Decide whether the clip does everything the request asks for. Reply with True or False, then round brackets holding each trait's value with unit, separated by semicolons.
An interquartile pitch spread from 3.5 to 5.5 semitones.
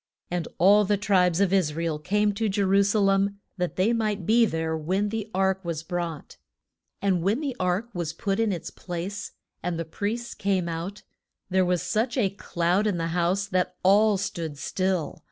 False (2.9 semitones)